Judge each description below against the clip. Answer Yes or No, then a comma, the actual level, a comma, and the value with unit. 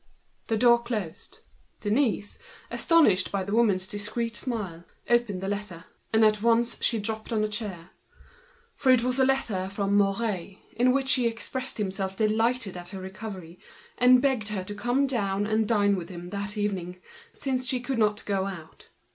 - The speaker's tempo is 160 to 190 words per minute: Yes, average, 165 wpm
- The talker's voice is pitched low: No, high, 210 Hz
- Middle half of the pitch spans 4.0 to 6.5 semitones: No, average, 3.6 semitones